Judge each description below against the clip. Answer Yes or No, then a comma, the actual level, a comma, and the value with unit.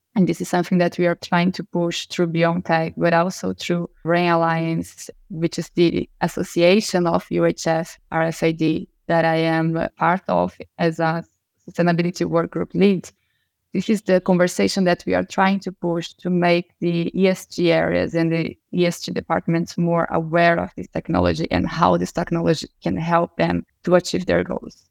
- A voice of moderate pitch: Yes, medium, 170 Hz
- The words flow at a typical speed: Yes, average, 170 wpm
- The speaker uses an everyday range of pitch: No, narrow, 1.3 semitones